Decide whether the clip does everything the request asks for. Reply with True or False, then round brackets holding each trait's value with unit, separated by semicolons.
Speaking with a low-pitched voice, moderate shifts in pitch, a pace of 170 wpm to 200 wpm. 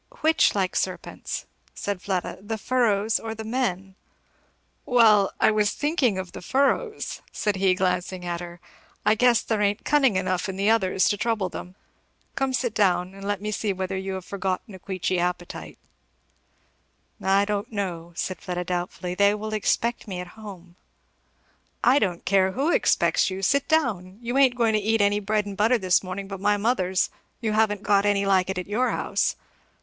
False (200 Hz; 3.0 semitones; 185 wpm)